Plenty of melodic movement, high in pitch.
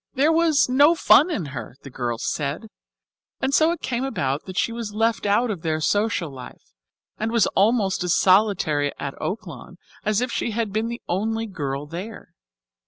Yes: wide, 7.0 semitones; high, 210 Hz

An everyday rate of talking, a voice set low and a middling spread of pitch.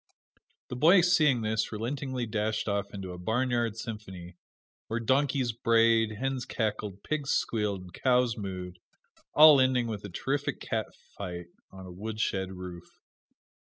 Yes: average, 145 wpm; low, 110 Hz; average, 4.5 semitones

